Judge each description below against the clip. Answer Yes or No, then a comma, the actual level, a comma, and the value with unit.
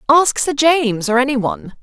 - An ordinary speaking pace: Yes, average, 165 wpm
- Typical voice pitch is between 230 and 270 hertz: Yes, very high, 265 Hz